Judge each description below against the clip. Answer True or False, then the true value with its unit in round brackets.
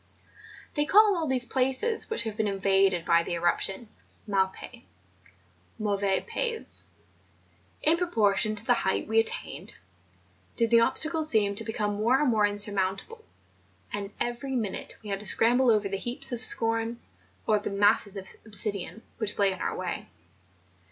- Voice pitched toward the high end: True (215 Hz)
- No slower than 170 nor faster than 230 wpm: False (160 wpm)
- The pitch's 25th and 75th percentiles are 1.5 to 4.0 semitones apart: True (3.7 semitones)